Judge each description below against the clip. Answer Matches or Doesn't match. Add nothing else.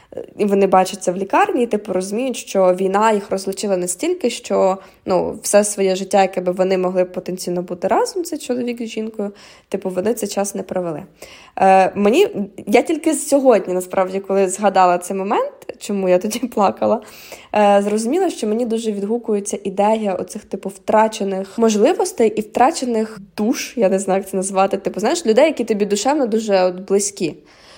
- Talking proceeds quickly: Matches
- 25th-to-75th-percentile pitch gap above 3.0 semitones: Matches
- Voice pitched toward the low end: Doesn't match